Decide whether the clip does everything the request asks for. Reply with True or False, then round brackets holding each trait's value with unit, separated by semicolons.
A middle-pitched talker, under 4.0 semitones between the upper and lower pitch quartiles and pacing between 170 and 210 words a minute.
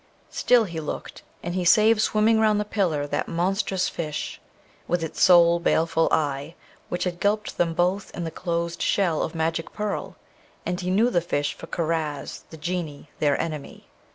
True (170 Hz; 3.1 semitones; 175 wpm)